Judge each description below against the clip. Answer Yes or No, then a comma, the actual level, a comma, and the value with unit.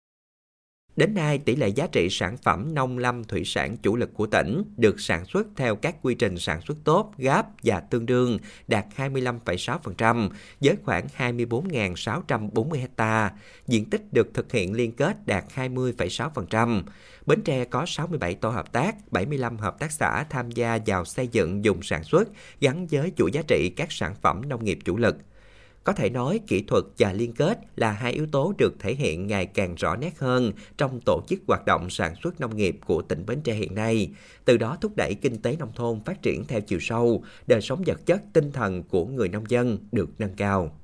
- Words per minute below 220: Yes, average, 200 wpm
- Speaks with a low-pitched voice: Yes, low, 120 Hz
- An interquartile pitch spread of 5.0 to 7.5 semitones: No, average, 4.0 semitones